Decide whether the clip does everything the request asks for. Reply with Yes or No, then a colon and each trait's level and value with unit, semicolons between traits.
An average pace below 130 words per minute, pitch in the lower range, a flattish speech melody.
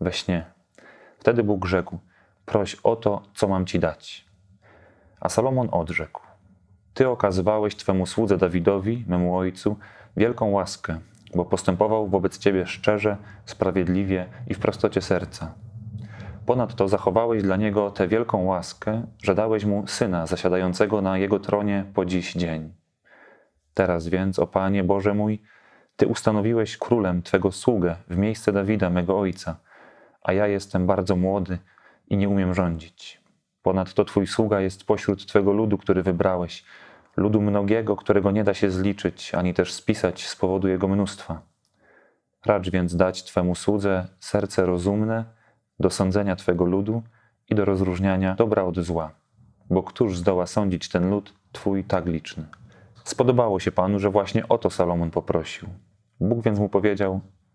No: average, 145 wpm; low, 100 Hz; narrow, 2.2 semitones